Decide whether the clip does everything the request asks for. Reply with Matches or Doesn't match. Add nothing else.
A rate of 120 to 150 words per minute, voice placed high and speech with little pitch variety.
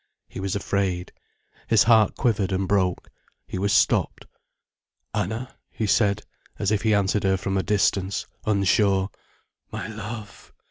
Doesn't match